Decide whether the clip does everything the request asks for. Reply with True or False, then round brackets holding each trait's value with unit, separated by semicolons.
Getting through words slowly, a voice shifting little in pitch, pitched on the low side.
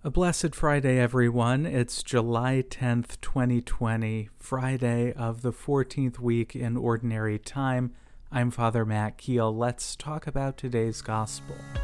True (125 wpm; 2.3 semitones; 120 Hz)